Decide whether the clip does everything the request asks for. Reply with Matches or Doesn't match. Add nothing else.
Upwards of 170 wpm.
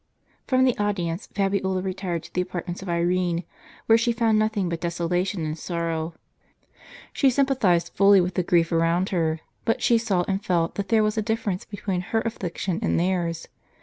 Matches